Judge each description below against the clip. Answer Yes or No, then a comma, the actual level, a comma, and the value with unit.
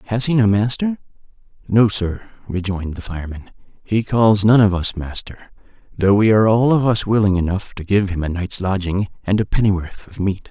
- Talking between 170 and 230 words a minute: Yes, average, 195 wpm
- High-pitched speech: No, low, 100 Hz